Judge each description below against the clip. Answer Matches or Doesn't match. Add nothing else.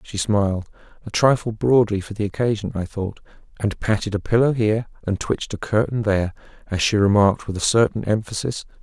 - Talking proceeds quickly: Doesn't match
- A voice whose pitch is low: Matches